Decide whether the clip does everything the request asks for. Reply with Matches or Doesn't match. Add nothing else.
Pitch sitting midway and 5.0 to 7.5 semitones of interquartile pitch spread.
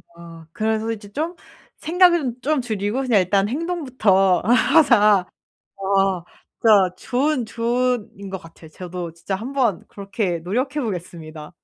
Doesn't match